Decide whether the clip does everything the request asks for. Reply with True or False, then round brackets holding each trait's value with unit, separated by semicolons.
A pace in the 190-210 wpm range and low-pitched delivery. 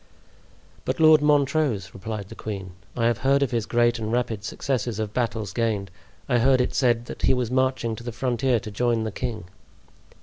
True (195 wpm; 120 Hz)